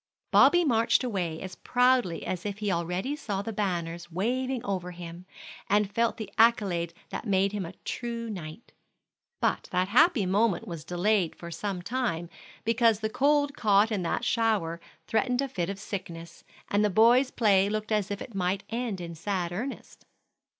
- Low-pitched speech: No, high, 205 Hz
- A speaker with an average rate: Yes, average, 170 wpm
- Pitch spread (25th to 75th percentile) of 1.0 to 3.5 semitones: No, average, 4.6 semitones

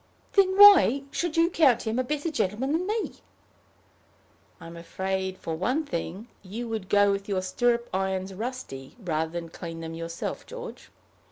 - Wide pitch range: Yes, wide, 7.4 semitones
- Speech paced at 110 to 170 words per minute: Yes, average, 160 wpm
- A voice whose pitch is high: Yes, high, 205 Hz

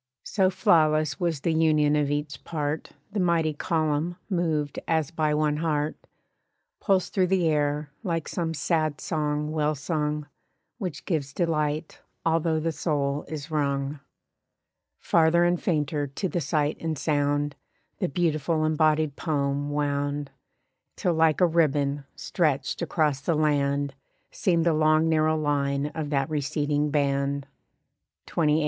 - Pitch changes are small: Yes, narrow, 2.0 semitones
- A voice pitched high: No, medium, 155 Hz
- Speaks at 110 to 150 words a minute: Yes, slow, 135 wpm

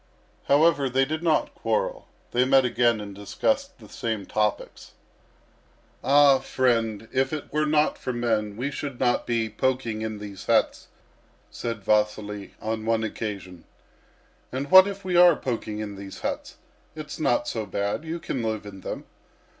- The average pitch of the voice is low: Yes, low, 120 Hz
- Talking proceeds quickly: No, average, 160 wpm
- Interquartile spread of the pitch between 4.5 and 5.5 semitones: Yes, average, 5.1 semitones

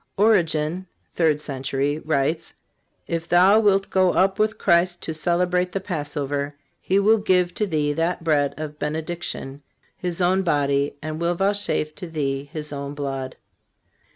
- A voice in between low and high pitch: Yes, medium, 165 Hz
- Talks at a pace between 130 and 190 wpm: Yes, average, 150 wpm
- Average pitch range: Yes, average, 3.9 semitones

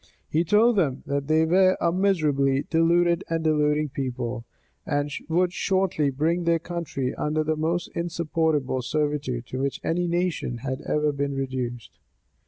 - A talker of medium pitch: Yes, medium, 155 Hz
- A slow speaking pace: No, average, 150 wpm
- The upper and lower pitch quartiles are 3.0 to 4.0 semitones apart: Yes, average, 3.7 semitones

